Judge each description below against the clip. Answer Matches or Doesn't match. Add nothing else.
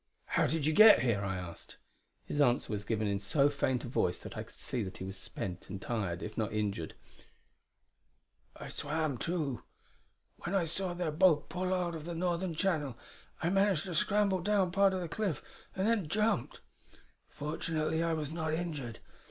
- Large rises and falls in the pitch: Matches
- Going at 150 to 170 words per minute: Doesn't match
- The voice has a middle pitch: Matches